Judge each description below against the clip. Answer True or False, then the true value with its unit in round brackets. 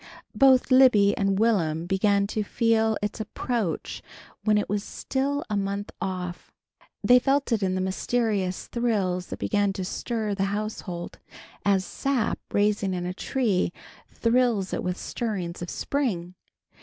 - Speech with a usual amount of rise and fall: True (3.7 semitones)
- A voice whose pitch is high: True (205 Hz)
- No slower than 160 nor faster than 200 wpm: False (145 wpm)